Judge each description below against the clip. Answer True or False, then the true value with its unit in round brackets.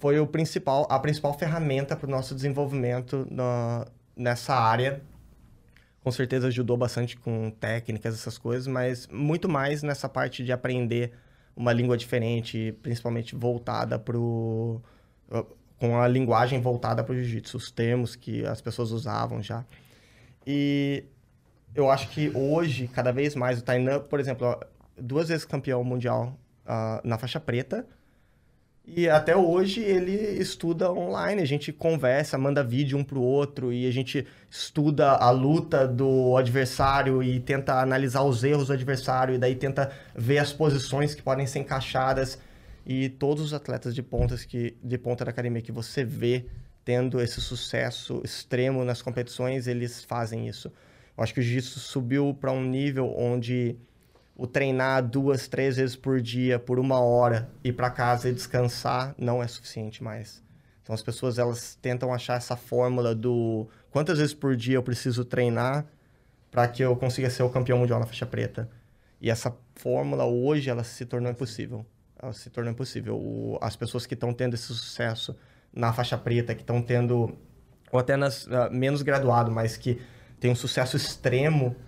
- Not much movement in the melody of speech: True (2.2 semitones)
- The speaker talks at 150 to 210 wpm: True (165 wpm)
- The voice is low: True (125 Hz)